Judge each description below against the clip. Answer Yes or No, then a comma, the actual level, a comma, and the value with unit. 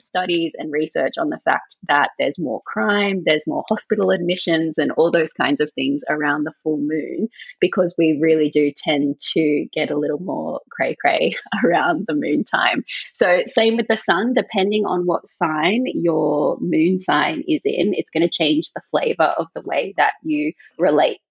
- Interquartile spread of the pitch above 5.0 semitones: Yes, wide, 5.5 semitones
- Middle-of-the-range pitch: Yes, medium, 170 Hz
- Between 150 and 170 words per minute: No, average, 185 wpm